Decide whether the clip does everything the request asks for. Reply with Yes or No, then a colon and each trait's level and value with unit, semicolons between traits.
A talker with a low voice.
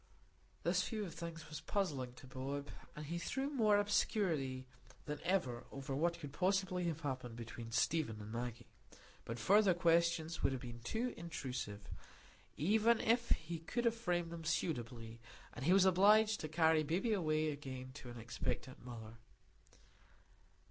No: medium, 160 Hz